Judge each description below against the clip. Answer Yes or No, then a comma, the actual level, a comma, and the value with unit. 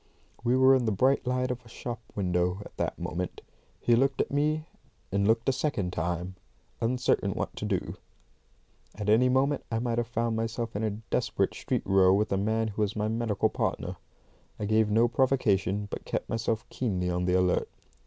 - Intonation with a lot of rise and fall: No, average, 3.8 semitones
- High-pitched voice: No, low, 110 Hz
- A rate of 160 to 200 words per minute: Yes, average, 195 wpm